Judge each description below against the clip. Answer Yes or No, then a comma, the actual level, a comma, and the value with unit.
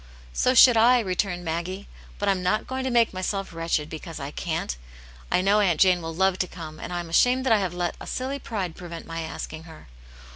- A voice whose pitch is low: No, medium, 180 Hz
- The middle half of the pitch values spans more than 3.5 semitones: Yes, average, 4.2 semitones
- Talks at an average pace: No, fast, 225 wpm